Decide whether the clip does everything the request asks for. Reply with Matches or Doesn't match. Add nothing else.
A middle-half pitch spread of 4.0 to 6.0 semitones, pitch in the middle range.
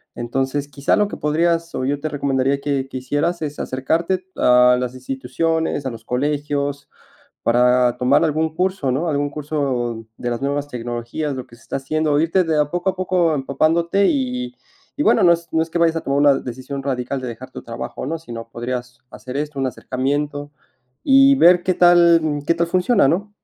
Matches